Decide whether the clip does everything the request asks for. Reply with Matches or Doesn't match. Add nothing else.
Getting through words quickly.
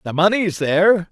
Doesn't match